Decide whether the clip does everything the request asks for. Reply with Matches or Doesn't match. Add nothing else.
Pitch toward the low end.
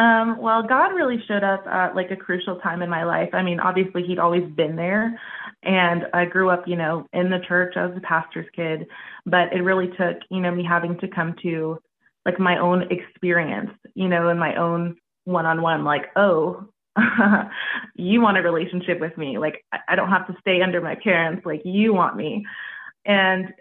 Doesn't match